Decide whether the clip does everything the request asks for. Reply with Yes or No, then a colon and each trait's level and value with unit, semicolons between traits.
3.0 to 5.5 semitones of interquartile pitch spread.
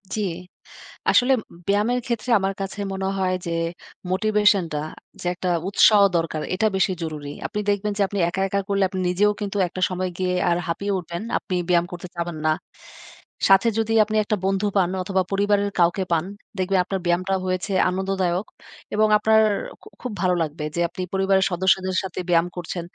No: narrow, 2.4 semitones